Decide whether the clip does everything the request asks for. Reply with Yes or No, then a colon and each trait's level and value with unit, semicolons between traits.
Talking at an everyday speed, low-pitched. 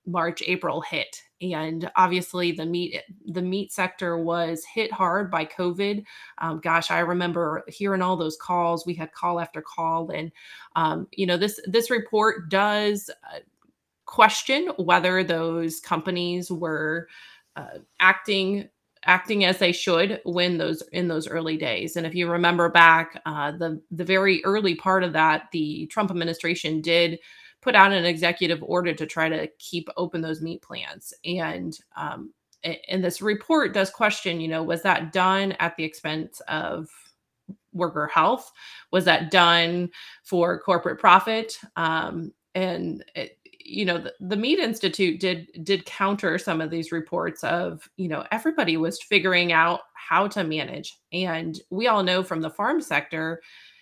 No: average, 155 wpm; medium, 175 Hz